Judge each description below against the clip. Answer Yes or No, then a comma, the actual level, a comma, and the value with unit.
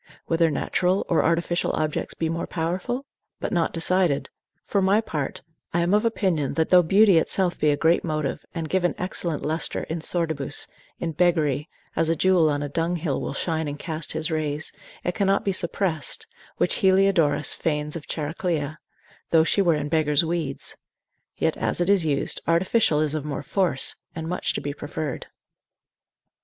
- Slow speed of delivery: No, average, 175 wpm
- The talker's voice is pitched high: No, medium, 165 Hz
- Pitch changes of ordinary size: Yes, average, 3.0 semitones